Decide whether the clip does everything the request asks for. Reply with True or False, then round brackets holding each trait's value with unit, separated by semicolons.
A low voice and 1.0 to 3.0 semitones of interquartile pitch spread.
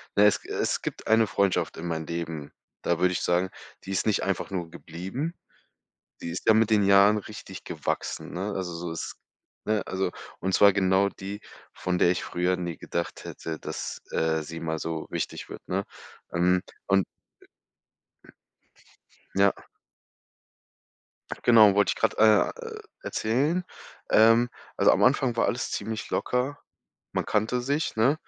False (95 Hz; 4.1 semitones)